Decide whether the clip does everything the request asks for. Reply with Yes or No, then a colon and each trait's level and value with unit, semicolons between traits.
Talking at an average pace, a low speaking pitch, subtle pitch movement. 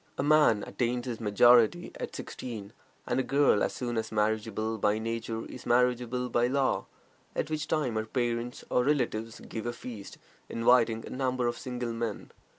Yes: average, 170 wpm; low, 120 Hz; narrow, 2.0 semitones